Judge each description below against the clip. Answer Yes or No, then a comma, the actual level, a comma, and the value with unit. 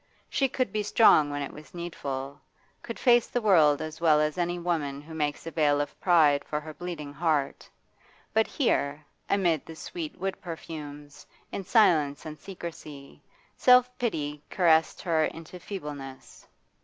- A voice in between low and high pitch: Yes, medium, 160 Hz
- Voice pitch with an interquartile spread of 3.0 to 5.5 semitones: Yes, average, 3.5 semitones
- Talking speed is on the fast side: No, average, 155 wpm